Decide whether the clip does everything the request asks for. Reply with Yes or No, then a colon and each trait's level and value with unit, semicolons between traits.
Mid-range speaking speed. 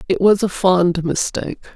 Yes: average, 170 wpm